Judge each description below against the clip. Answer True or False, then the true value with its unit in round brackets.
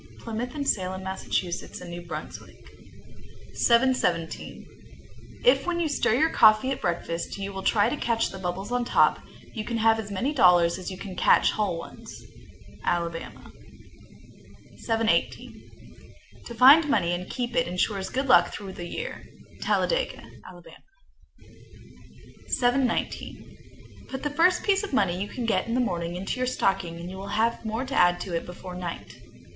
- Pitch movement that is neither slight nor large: False (5.9 semitones)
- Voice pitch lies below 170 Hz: False (215 Hz)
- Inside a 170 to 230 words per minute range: False (160 wpm)